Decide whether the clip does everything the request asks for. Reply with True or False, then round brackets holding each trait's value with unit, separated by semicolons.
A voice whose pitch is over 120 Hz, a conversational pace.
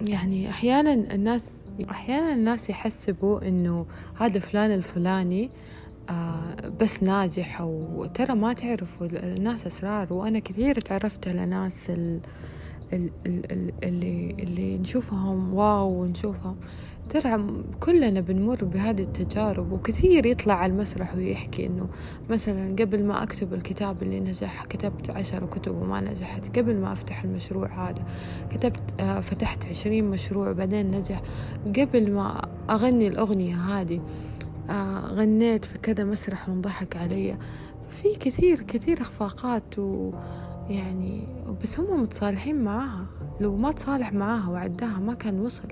True (190 Hz; 120 wpm)